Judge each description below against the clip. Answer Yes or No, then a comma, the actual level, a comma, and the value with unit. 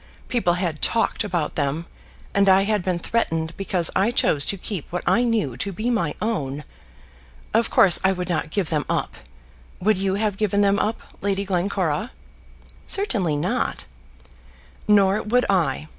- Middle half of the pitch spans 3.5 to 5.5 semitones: Yes, average, 4.0 semitones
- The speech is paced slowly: No, average, 160 wpm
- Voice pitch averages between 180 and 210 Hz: Yes, high, 190 Hz